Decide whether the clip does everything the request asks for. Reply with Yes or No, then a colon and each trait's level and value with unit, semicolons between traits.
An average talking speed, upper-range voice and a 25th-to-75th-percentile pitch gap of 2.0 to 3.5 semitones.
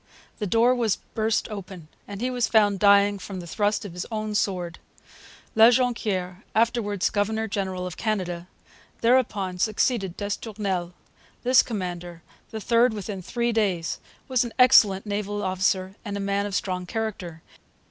Yes: average, 150 wpm; high, 205 Hz; average, 3.0 semitones